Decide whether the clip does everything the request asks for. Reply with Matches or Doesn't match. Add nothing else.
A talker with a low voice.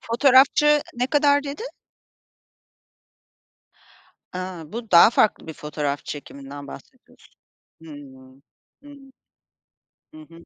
Doesn't match